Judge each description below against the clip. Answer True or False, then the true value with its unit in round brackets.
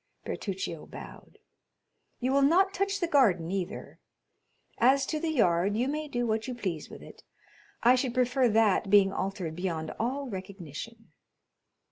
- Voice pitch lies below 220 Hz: False (230 Hz)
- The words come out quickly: False (150 wpm)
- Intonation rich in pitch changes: True (6.0 semitones)